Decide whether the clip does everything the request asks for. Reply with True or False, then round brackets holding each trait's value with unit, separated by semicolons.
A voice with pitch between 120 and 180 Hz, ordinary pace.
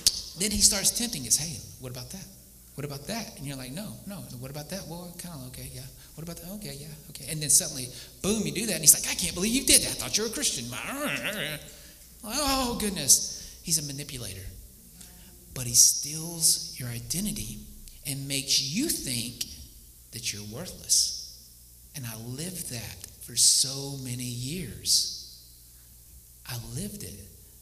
True (135 Hz; 175 wpm)